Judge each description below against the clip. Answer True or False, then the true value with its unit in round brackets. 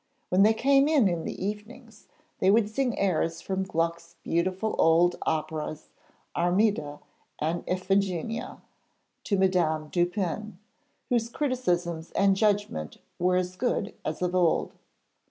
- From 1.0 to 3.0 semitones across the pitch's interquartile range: False (4.0 semitones)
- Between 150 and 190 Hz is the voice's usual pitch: True (185 Hz)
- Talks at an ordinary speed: False (120 wpm)